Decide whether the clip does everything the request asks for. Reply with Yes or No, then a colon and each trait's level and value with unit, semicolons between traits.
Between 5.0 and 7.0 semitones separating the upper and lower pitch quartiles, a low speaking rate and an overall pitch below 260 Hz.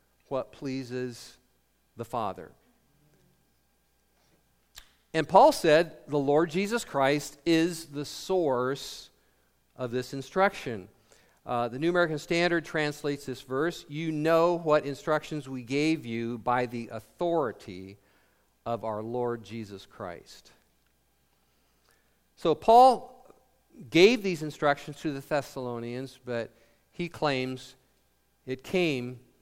Yes: wide, 5.4 semitones; slow, 110 wpm; low, 135 Hz